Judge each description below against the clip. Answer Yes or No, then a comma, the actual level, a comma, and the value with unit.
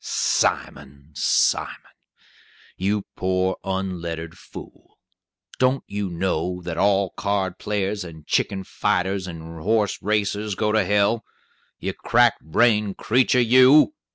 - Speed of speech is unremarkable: No, slow, 115 wpm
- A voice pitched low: Yes, very low, 95 Hz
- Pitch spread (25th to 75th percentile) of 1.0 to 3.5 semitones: Yes, average, 2.9 semitones